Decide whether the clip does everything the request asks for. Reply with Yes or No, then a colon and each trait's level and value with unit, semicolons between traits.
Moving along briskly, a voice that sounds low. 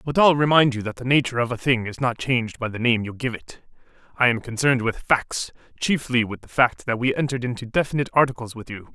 Yes: fast, 240 wpm; low, 125 Hz